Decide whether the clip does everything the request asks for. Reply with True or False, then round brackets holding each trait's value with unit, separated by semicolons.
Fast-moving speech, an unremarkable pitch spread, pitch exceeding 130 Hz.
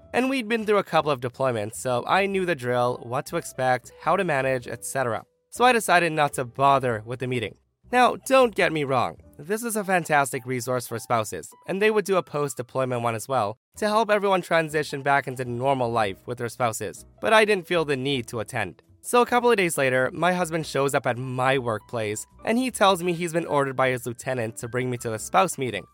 False (230 wpm; 6.7 semitones; 140 Hz)